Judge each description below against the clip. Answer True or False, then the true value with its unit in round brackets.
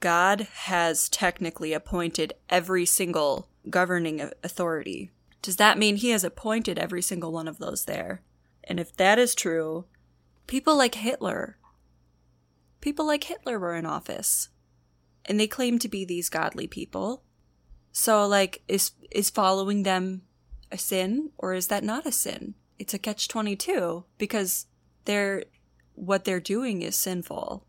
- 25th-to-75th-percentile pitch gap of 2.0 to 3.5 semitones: False (4.3 semitones)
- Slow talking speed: False (145 wpm)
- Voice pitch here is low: False (185 Hz)